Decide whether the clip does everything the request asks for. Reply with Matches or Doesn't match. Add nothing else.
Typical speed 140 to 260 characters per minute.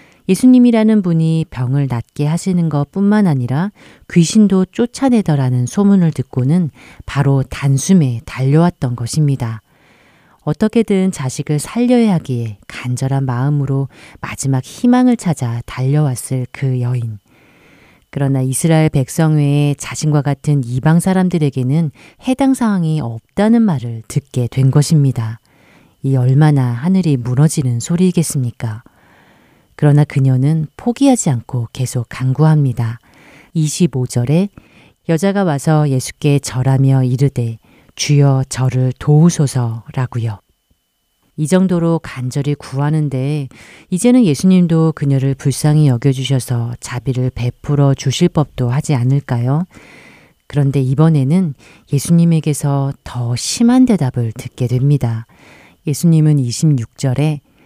Doesn't match